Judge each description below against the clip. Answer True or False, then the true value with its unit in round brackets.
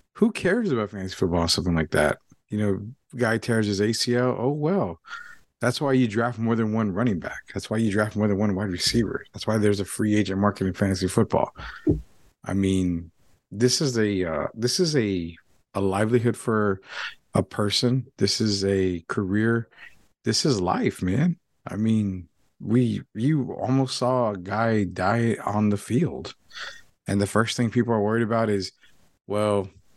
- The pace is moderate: True (180 wpm)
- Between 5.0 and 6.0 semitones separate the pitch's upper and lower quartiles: False (3.7 semitones)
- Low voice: True (105 Hz)